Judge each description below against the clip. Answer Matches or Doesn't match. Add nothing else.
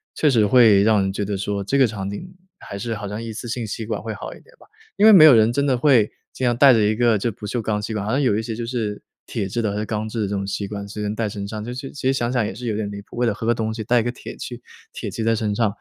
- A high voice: Doesn't match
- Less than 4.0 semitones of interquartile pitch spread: Matches